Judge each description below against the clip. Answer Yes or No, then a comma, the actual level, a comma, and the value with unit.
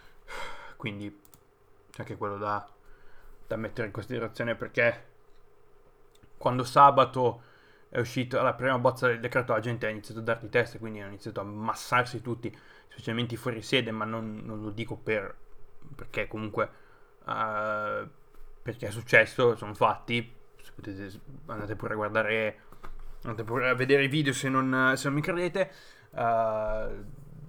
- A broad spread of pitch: No, average, 3.5 semitones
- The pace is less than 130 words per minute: No, average, 145 wpm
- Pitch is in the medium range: No, low, 115 Hz